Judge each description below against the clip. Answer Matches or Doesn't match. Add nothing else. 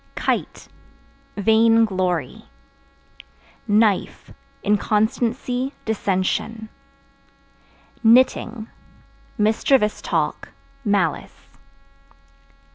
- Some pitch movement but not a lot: Doesn't match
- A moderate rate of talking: Doesn't match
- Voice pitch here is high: Matches